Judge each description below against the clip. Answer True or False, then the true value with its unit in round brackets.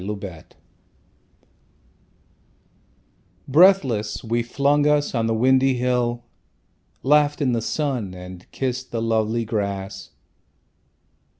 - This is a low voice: True (120 Hz)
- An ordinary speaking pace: False (100 wpm)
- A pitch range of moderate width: True (3.8 semitones)